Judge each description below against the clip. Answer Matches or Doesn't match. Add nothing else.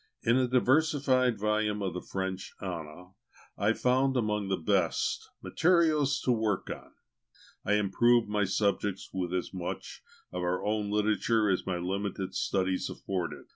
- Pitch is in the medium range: Doesn't match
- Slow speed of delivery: Doesn't match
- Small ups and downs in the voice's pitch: Doesn't match